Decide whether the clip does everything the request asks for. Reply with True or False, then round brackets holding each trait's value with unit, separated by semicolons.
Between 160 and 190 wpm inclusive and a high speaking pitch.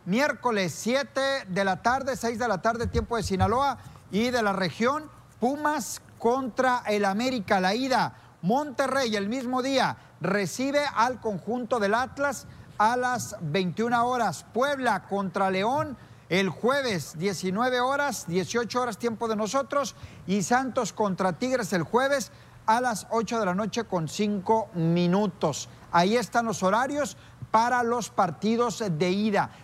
False (145 wpm; 225 Hz)